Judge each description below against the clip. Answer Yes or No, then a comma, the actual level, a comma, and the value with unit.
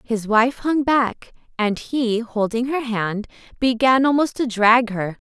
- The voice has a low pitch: No, high, 235 Hz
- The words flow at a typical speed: Yes, average, 160 wpm